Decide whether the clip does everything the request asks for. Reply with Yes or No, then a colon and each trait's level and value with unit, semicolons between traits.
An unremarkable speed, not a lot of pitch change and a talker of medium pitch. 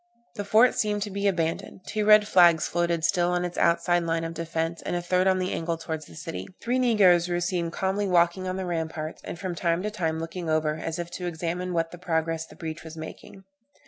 No: fast, 225 wpm; narrow, 2.3 semitones; medium, 175 Hz